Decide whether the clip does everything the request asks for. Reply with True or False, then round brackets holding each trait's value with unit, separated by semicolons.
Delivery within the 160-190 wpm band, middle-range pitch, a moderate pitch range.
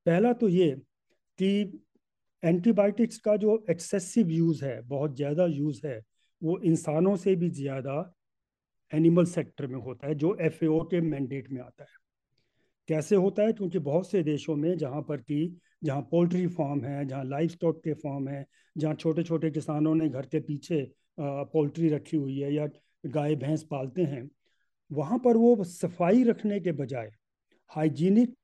True (165 wpm; 160 Hz; 3.9 semitones)